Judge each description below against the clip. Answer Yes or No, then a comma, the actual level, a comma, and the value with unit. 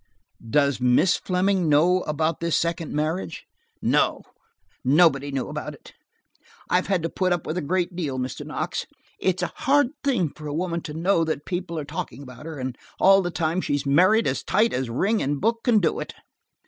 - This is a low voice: No, medium, 165 Hz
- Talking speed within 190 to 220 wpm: Yes, average, 200 wpm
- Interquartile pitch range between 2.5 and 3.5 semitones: No, average, 4.2 semitones